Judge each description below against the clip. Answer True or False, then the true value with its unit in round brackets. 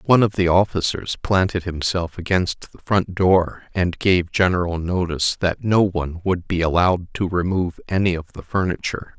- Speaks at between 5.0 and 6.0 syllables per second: True (5.1 syllables/s)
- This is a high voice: False (90 Hz)